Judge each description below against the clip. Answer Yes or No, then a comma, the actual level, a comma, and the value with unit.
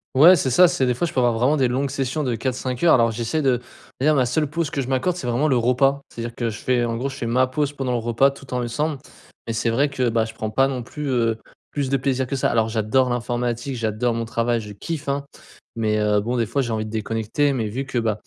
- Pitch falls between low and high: No, low, 125 Hz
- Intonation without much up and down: No, average, 3.0 semitones